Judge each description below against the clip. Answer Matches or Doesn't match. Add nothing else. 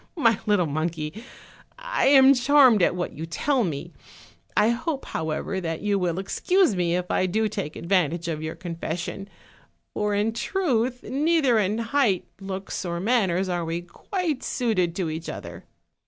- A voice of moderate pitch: Doesn't match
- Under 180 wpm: Matches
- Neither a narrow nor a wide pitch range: Doesn't match